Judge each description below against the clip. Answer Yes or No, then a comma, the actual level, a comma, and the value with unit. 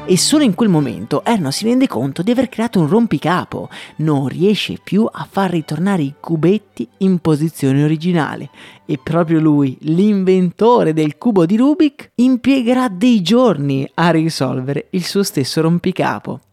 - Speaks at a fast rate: No, average, 150 wpm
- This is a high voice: No, medium, 175 Hz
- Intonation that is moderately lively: No, wide, 6.5 semitones